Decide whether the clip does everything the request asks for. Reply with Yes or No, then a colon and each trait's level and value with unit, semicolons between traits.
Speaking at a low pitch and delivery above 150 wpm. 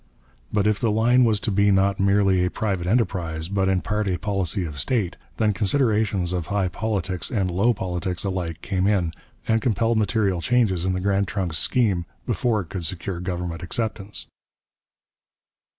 Yes: very low, 95 Hz; average, 170 wpm